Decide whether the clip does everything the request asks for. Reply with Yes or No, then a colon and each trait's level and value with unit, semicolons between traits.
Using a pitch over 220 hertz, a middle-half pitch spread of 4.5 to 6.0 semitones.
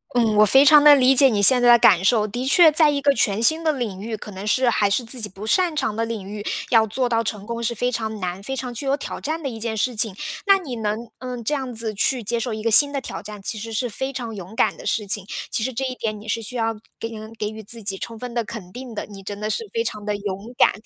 No: high, 230 Hz; average, 3.5 semitones